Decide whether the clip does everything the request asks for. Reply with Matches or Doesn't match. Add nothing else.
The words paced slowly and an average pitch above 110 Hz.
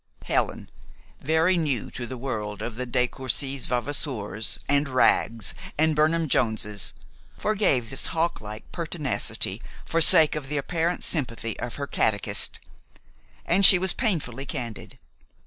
Matches